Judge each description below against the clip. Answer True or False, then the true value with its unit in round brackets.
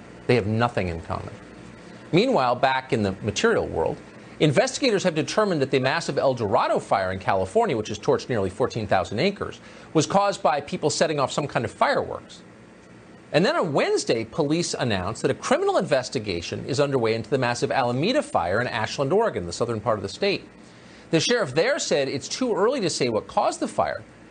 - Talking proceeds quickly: False (190 wpm)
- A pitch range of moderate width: False (7.2 semitones)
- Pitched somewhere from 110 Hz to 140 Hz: True (135 Hz)